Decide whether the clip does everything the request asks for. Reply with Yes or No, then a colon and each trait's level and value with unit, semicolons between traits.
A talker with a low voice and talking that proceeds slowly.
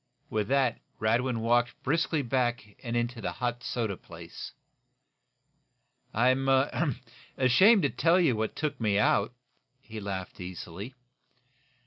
Yes: low, 120 Hz; slow, 120 wpm